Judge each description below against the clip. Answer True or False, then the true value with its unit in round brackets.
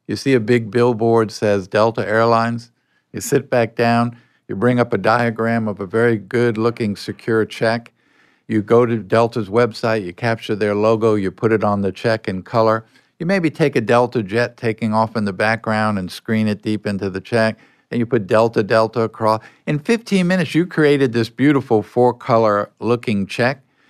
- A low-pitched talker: True (115 Hz)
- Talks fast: False (185 wpm)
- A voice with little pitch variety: True (1.9 semitones)